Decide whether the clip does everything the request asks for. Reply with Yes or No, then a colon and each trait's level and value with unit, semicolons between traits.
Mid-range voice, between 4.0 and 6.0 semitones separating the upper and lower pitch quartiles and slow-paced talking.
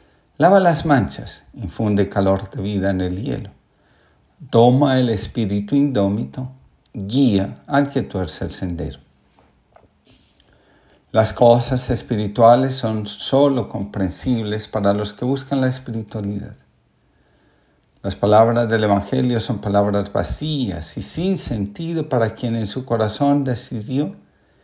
No: low, 110 Hz; average, 4.4 semitones; slow, 115 wpm